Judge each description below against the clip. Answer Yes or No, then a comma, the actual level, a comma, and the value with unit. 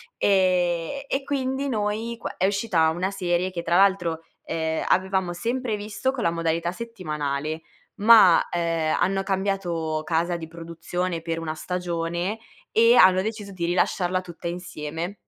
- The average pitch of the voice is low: No, medium, 180 Hz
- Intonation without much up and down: No, average, 3.3 semitones